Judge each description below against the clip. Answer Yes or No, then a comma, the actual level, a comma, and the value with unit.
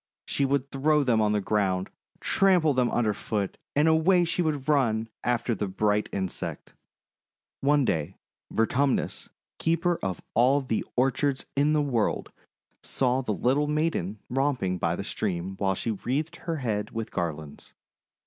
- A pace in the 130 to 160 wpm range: Yes, average, 155 wpm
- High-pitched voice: No, low, 125 Hz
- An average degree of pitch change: No, wide, 6.0 semitones